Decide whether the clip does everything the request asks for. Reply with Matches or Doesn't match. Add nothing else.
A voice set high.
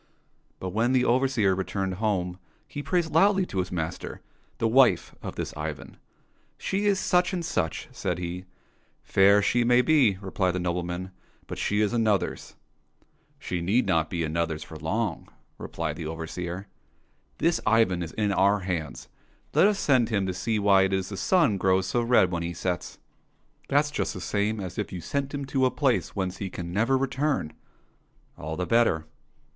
Doesn't match